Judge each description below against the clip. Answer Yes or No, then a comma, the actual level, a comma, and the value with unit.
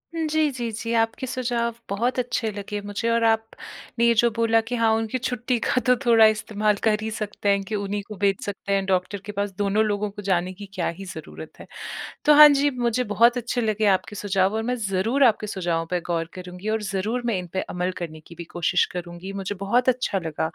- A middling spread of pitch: Yes, average, 3.3 semitones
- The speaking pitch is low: No, high, 215 Hz